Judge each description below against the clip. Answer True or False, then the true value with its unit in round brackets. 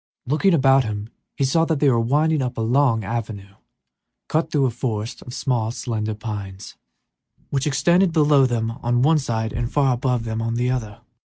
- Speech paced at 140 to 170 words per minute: False (180 wpm)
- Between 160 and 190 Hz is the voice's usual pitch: False (125 Hz)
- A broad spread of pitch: False (4.0 semitones)